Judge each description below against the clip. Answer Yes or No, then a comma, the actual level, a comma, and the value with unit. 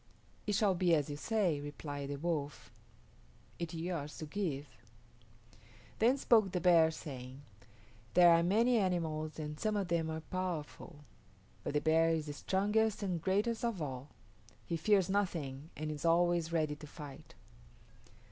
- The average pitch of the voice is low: No, medium, 165 Hz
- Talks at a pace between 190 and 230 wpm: No, average, 155 wpm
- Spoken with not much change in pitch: No, average, 4.1 semitones